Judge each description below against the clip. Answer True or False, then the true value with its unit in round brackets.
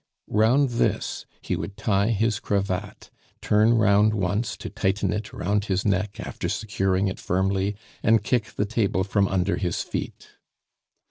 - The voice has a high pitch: False (100 Hz)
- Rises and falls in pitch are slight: True (2.1 semitones)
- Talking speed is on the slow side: False (150 wpm)